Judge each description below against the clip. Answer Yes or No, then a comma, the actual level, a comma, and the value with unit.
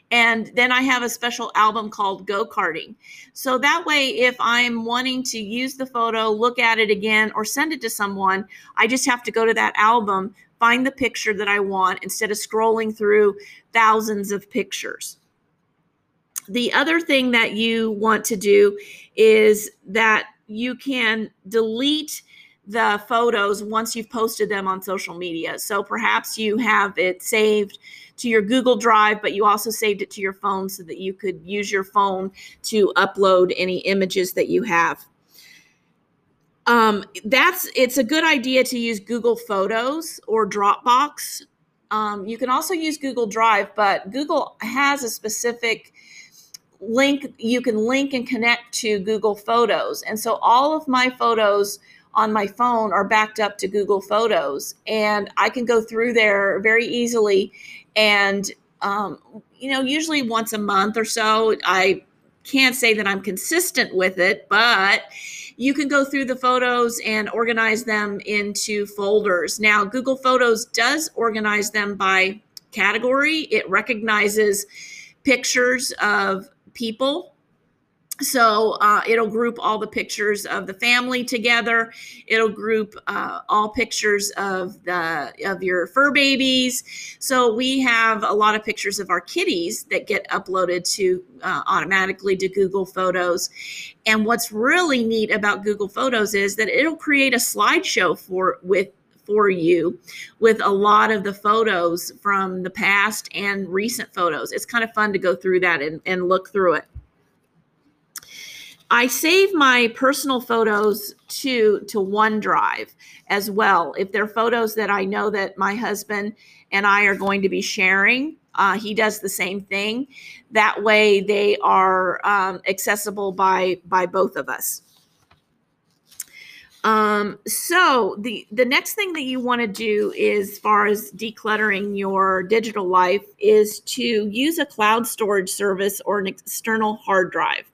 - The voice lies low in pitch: No, high, 215 Hz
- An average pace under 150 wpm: No, average, 155 wpm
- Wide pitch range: No, average, 3.1 semitones